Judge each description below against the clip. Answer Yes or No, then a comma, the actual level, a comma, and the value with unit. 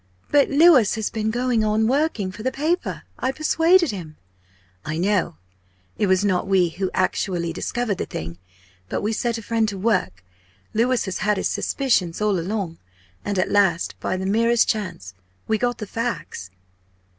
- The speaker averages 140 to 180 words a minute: Yes, average, 170 wpm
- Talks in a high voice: Yes, high, 210 Hz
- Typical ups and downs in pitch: Yes, average, 4.3 semitones